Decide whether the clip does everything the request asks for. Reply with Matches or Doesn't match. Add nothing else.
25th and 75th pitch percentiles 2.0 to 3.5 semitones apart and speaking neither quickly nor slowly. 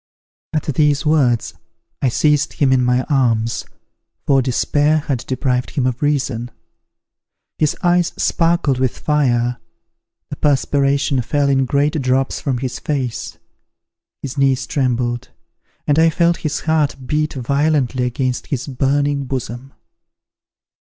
Doesn't match